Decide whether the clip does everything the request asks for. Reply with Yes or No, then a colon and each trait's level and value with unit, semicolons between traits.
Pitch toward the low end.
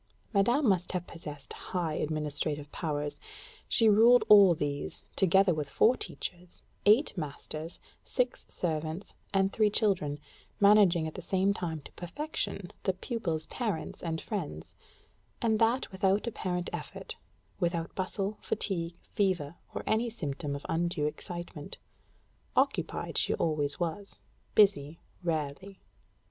No: medium, 175 Hz